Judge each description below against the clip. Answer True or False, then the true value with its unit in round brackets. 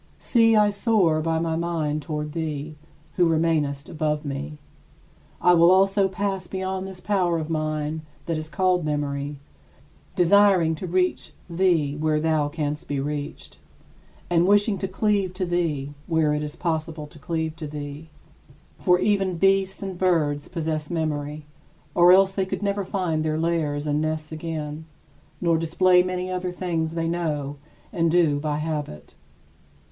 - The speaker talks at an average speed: True (155 wpm)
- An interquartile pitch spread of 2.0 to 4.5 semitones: True (3.2 semitones)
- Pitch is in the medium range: True (165 Hz)